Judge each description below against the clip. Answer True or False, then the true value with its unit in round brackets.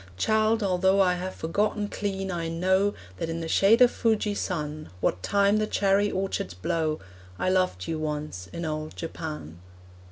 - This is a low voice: False (185 Hz)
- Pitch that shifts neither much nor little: True (4.5 semitones)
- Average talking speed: True (160 wpm)